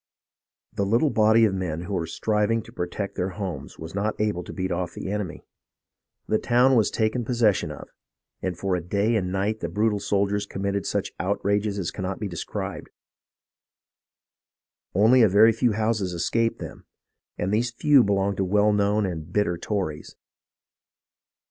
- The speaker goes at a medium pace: Yes, average, 165 wpm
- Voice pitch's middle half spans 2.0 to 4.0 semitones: Yes, average, 2.8 semitones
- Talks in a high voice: No, low, 100 Hz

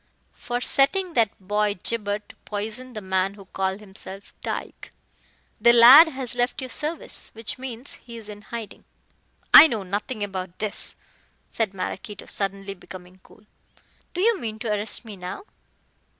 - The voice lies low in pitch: No, high, 215 Hz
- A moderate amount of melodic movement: Yes, average, 3.7 semitones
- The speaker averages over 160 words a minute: No, average, 155 wpm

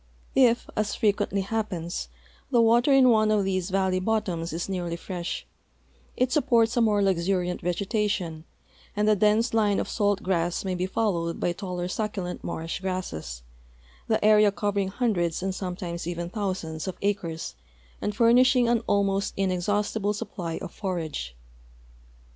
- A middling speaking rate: Yes, average, 150 wpm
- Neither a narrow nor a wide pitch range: Yes, average, 3.4 semitones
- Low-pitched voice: No, high, 195 Hz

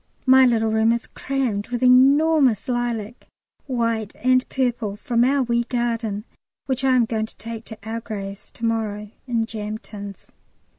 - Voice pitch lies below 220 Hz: No, high, 230 Hz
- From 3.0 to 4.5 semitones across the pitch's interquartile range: No, narrow, 2.5 semitones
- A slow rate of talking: No, average, 160 wpm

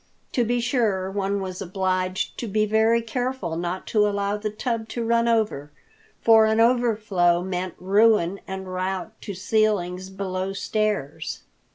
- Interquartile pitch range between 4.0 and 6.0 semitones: No, average, 3.1 semitones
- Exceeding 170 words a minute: No, average, 150 wpm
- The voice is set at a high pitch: Yes, high, 200 Hz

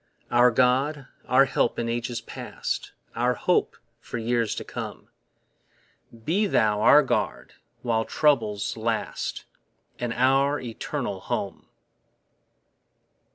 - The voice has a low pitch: Yes, low, 120 Hz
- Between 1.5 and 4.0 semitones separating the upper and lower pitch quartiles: Yes, average, 3.0 semitones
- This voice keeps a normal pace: No, slow, 110 wpm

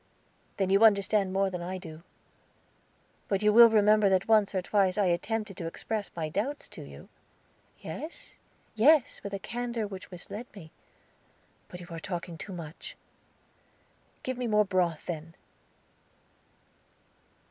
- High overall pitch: Yes, high, 195 Hz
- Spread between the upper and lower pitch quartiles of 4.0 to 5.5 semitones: No, average, 3.3 semitones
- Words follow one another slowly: No, average, 145 wpm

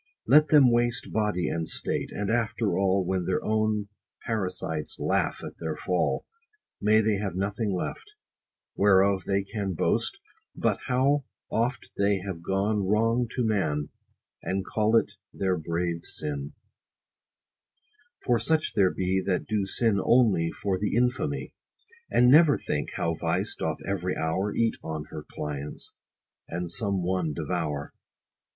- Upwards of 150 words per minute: No, average, 145 wpm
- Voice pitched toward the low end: Yes, low, 100 Hz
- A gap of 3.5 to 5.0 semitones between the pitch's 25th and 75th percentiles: Yes, average, 4.0 semitones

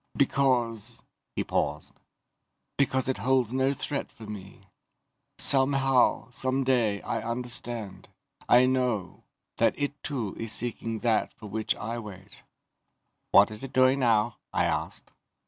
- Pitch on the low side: Yes, low, 120 Hz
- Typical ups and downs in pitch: Yes, average, 3.3 semitones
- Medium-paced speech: No, slow, 130 wpm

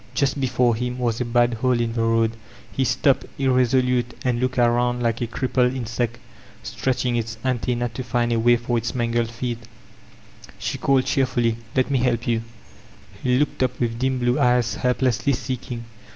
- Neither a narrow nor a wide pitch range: No, narrow, 1.4 semitones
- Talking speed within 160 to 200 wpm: Yes, average, 180 wpm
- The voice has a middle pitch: No, low, 120 Hz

